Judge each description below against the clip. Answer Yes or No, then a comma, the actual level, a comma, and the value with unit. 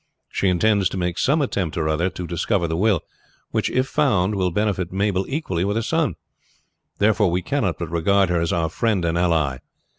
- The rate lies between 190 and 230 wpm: Yes, average, 200 wpm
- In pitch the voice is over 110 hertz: No, very low, 95 Hz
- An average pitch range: Yes, average, 3.8 semitones